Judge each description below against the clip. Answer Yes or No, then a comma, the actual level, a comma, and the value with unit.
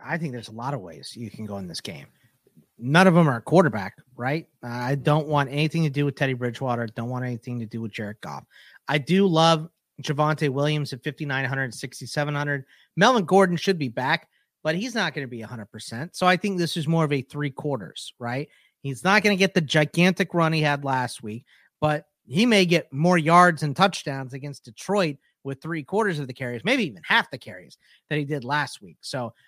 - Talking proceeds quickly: Yes, fast, 215 wpm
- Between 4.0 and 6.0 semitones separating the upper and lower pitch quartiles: Yes, average, 4.5 semitones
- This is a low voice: No, medium, 150 Hz